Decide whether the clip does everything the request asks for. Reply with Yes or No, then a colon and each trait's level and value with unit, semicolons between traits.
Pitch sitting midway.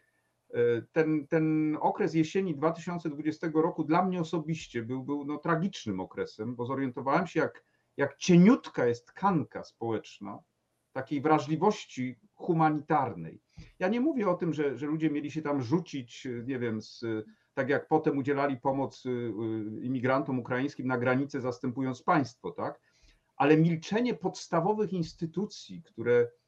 Yes: medium, 150 Hz